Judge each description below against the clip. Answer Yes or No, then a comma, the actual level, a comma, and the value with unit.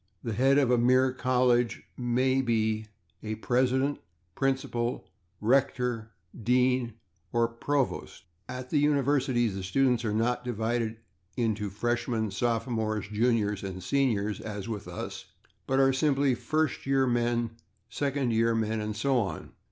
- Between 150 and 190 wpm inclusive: No, slow, 135 wpm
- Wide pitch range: No, average, 2.9 semitones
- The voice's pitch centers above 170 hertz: No, low, 120 Hz